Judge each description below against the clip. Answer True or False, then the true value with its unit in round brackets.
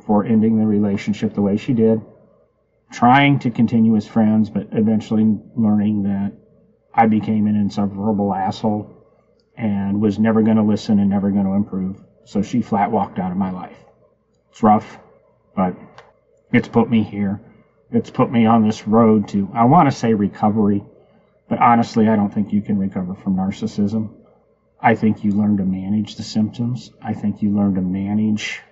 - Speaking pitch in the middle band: False (110 Hz)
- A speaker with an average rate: True (175 wpm)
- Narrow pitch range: True (2.1 semitones)